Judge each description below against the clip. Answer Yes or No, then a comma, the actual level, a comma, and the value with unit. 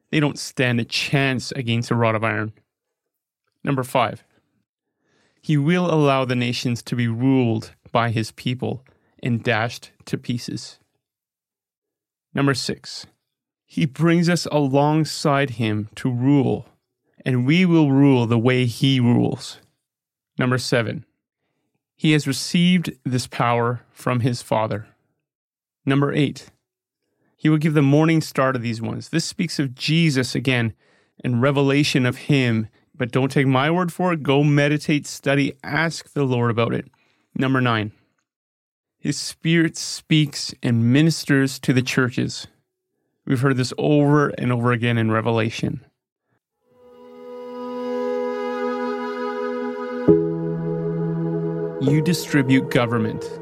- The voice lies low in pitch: Yes, low, 130 Hz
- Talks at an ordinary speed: No, slow, 125 wpm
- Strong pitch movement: No, average, 4.2 semitones